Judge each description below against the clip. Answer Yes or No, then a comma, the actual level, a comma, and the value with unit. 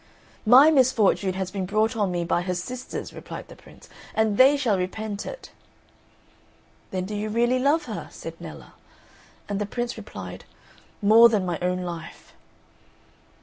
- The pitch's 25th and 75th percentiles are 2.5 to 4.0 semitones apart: No, average, 4.7 semitones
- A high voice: Yes, high, 210 Hz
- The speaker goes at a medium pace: Yes, average, 155 wpm